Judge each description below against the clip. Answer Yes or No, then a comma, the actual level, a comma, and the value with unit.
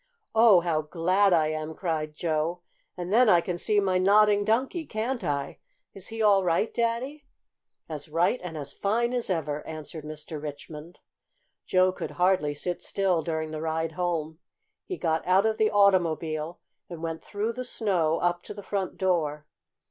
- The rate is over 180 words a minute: No, average, 170 wpm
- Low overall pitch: No, medium, 175 Hz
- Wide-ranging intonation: No, average, 4.4 semitones